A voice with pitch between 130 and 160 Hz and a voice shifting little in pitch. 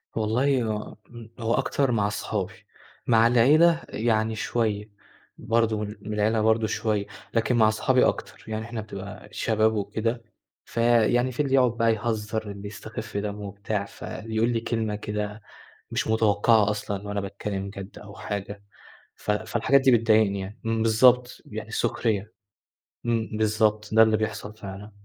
No: low, 110 Hz; narrow, 1.8 semitones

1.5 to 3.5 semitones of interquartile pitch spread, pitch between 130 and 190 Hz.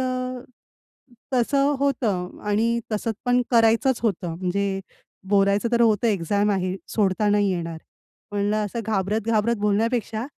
No: average, 2.9 semitones; high, 210 Hz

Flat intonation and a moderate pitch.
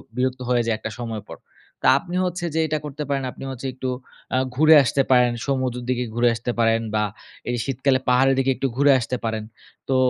No: narrow, 2.2 semitones; low, 130 Hz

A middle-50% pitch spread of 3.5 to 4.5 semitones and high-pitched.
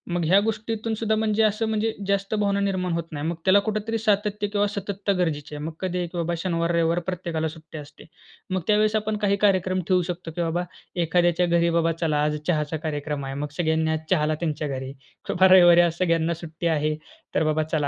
No: average, 4.0 semitones; medium, 175 Hz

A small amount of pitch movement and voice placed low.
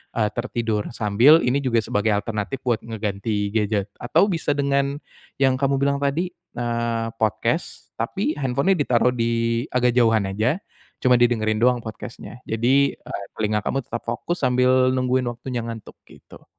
No: average, 3.2 semitones; low, 120 Hz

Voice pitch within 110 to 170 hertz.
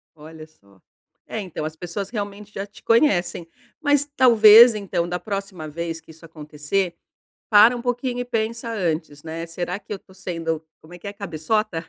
No: medium, 185 Hz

